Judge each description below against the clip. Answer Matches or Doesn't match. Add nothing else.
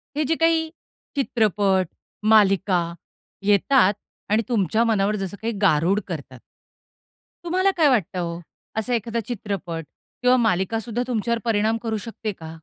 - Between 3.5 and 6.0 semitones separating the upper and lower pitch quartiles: Matches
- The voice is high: Matches